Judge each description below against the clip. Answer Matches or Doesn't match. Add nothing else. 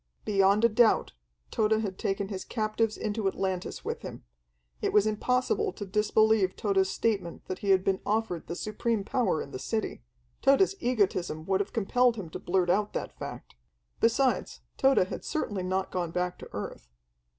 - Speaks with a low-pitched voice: Doesn't match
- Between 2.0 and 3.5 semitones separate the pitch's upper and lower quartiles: Matches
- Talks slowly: Doesn't match